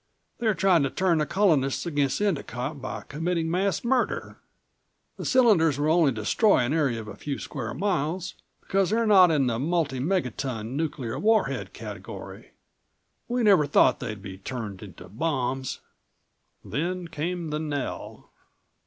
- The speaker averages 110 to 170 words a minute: Yes, average, 145 wpm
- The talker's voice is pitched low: No, medium, 155 Hz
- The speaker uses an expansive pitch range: Yes, wide, 5.8 semitones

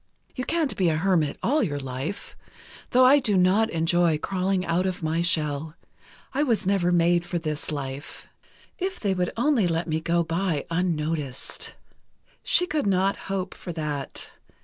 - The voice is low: No, medium, 175 Hz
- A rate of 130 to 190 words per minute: Yes, average, 160 wpm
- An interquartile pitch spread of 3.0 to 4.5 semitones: Yes, average, 3.8 semitones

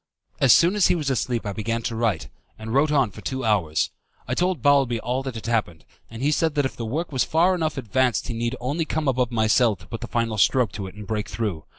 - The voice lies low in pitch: Yes, low, 120 Hz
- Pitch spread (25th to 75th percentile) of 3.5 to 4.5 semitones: Yes, average, 4.2 semitones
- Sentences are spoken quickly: Yes, fast, 255 wpm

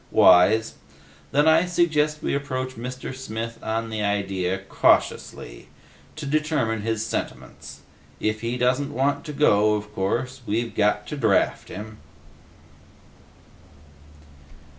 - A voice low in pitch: Yes, low, 115 Hz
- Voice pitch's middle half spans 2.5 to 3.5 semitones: No, average, 4.9 semitones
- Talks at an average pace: No, slow, 120 wpm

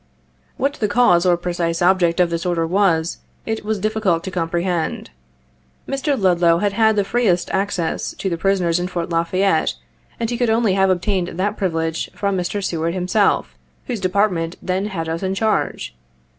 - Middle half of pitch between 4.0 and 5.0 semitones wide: No, average, 3.2 semitones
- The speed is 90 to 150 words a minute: No, average, 175 wpm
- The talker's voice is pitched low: No, medium, 185 Hz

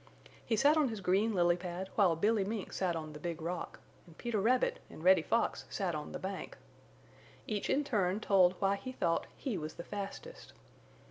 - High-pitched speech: Yes, high, 195 Hz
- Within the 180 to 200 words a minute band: Yes, average, 195 wpm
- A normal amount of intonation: Yes, average, 4.1 semitones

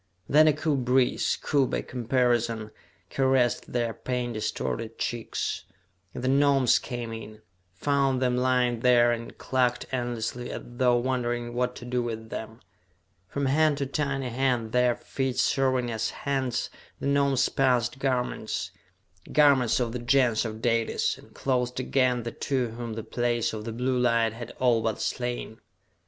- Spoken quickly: No, average, 155 wpm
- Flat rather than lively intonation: Yes, narrow, 2.0 semitones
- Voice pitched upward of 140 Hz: No, low, 125 Hz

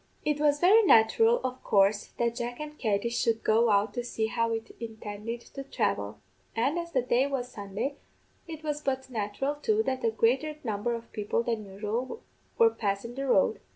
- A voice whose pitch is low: No, high, 235 Hz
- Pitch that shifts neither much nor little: Yes, average, 4.2 semitones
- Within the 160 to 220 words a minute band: Yes, average, 190 wpm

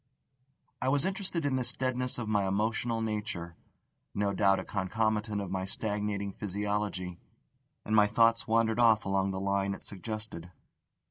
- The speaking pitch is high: No, low, 105 Hz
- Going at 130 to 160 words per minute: Yes, average, 150 wpm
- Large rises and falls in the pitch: No, average, 2.7 semitones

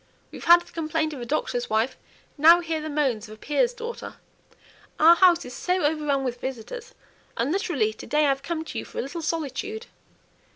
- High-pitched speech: Yes, very high, 305 Hz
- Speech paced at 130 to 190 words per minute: No, fast, 205 wpm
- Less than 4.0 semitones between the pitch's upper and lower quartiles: No, average, 4.7 semitones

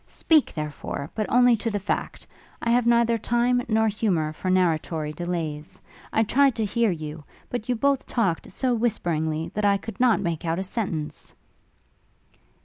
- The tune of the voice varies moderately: No, wide, 6.4 semitones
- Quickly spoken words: No, average, 165 wpm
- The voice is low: No, high, 205 Hz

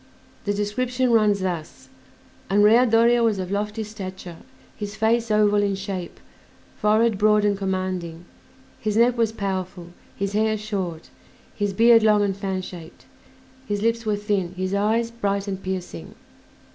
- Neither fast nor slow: Yes, average, 145 wpm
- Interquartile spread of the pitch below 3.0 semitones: Yes, narrow, 2.5 semitones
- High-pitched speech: Yes, high, 205 Hz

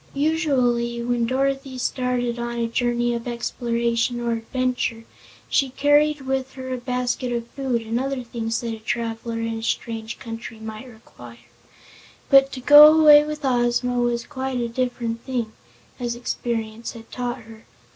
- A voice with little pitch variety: Yes, narrow, 2.0 semitones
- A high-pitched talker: Yes, high, 240 Hz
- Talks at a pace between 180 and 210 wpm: No, average, 155 wpm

